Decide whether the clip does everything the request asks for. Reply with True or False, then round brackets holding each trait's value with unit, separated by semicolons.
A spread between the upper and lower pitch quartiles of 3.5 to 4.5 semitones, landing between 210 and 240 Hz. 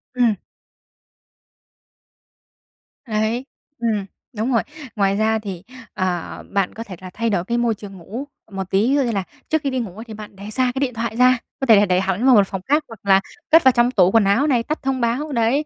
True (4.1 semitones; 225 Hz)